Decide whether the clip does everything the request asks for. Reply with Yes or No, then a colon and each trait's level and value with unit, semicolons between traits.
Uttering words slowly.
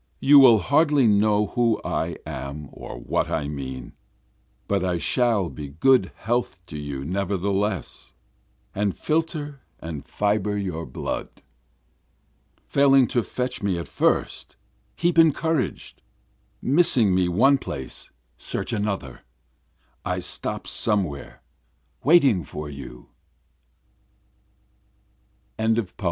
Yes: slow, 110 wpm